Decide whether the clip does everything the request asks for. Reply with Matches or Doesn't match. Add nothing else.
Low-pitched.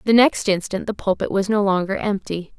Doesn't match